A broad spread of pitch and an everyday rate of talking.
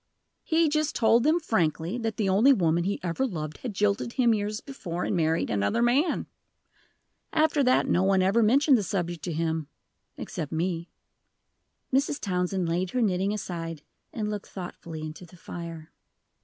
Yes: wide, 5.9 semitones; average, 165 wpm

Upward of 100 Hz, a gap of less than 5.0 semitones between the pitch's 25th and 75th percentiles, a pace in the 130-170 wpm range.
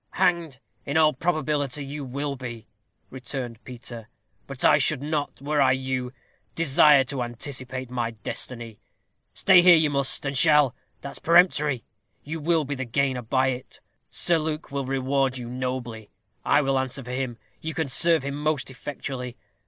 Yes: low, 135 Hz; average, 2.9 semitones; average, 160 wpm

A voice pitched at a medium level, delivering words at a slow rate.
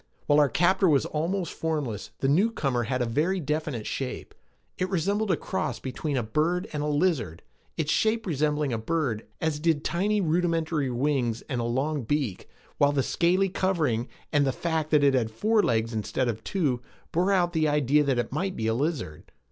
No: medium, 150 Hz; average, 190 wpm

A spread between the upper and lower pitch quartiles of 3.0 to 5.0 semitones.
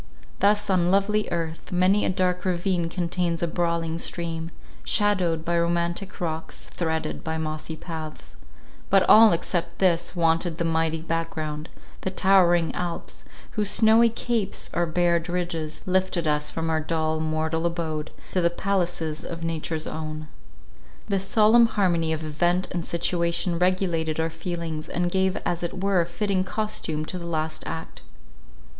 No: narrow, 2.4 semitones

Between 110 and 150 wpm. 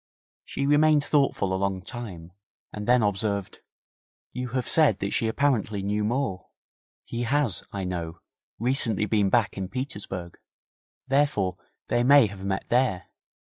Yes: average, 140 wpm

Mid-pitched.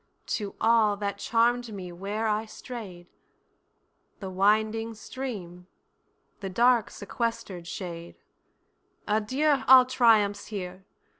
No: high, 210 Hz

